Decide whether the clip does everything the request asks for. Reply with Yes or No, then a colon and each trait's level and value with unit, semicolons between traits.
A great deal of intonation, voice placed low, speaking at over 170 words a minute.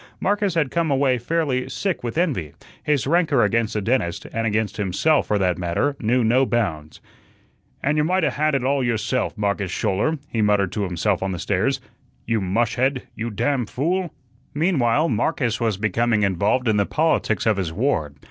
Yes: wide, 5.8 semitones; low, 120 Hz; average, 180 wpm